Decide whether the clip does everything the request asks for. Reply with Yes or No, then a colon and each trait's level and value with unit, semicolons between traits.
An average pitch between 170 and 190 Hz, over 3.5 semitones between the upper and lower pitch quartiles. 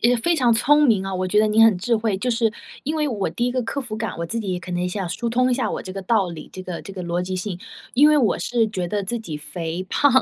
No: high, 215 Hz; average, 4.7 semitones